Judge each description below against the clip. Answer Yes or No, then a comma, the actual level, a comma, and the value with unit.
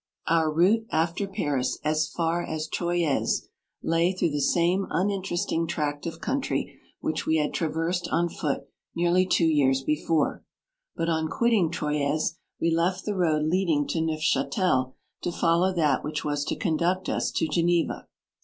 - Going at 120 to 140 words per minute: No, average, 165 wpm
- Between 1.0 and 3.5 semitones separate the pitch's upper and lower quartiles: Yes, narrow, 2.5 semitones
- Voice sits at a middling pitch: Yes, medium, 165 Hz